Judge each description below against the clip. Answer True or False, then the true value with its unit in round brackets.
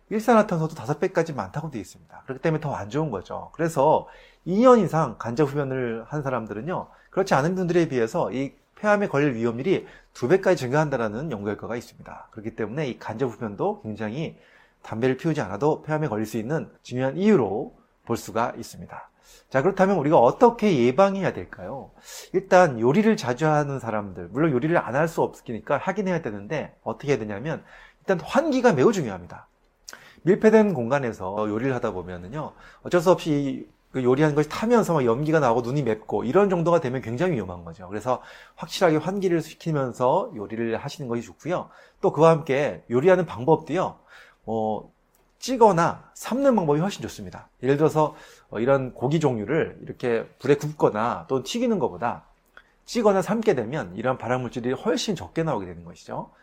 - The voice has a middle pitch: True (150 Hz)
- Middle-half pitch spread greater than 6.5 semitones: True (7.4 semitones)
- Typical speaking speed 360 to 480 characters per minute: True (385 characters per minute)